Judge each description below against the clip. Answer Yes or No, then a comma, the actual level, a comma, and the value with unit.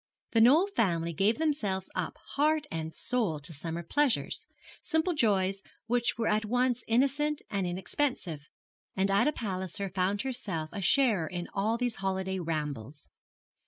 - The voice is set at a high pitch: Yes, high, 200 Hz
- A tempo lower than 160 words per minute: Yes, average, 145 wpm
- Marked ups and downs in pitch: Yes, wide, 6.0 semitones